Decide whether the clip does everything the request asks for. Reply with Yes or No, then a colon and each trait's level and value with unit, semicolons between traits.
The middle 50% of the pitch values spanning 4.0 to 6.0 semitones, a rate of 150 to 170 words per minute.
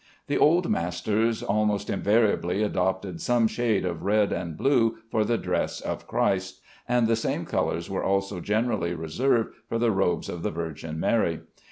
Yes: average, 4.3 semitones; average, 165 wpm